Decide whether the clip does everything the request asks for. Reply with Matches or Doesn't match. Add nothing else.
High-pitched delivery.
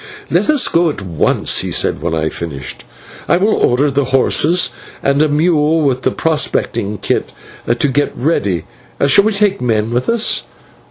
Doesn't match